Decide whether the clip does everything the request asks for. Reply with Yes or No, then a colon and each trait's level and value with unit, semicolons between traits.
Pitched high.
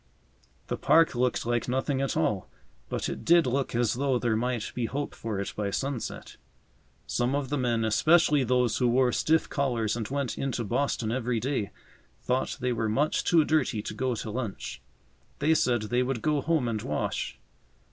No: low, 125 Hz